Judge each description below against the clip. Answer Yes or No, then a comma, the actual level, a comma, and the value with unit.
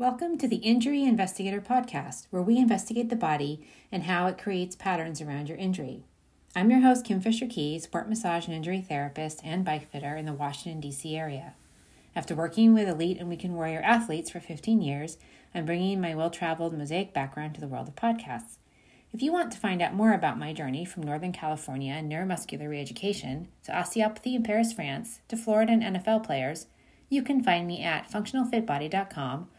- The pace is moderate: Yes, average, 185 wpm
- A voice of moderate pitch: Yes, medium, 180 Hz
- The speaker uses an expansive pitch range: Yes, wide, 6.2 semitones